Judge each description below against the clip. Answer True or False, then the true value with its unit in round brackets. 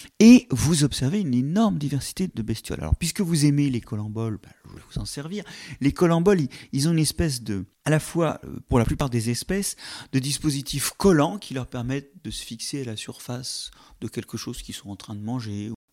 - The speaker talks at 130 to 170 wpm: False (210 wpm)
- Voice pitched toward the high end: False (135 Hz)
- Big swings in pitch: True (5.8 semitones)